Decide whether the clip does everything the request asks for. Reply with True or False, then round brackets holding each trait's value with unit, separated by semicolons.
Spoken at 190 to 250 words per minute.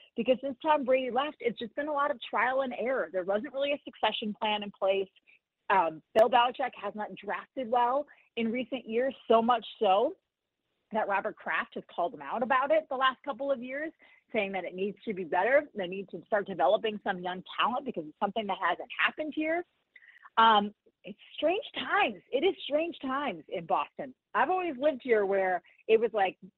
True (200 wpm)